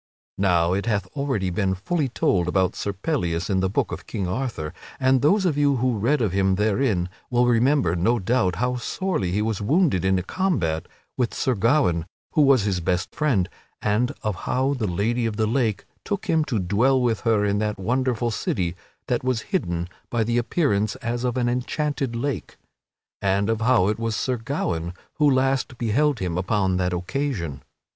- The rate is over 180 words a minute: Yes, average, 190 wpm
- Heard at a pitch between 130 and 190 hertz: No, low, 115 Hz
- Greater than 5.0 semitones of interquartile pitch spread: Yes, wide, 5.5 semitones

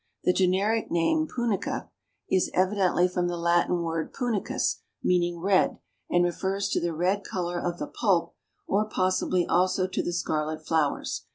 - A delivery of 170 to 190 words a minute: No, average, 155 wpm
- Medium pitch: Yes, medium, 180 Hz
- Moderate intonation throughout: No, narrow, 2.1 semitones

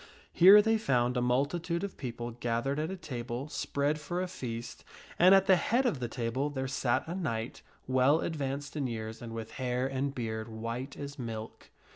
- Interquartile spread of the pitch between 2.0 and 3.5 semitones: No, average, 4.7 semitones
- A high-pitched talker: No, low, 135 Hz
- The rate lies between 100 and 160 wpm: No, average, 190 wpm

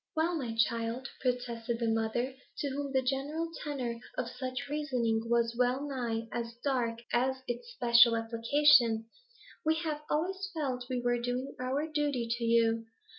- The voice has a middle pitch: No, very high, 250 Hz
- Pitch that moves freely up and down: No, average, 3.3 semitones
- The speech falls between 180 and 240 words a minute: No, average, 155 wpm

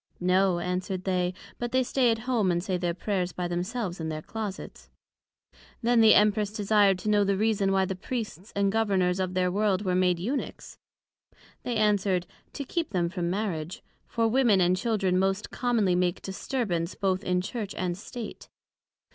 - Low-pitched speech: No, high, 195 Hz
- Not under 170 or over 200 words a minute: Yes, average, 175 wpm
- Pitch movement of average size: Yes, average, 3.2 semitones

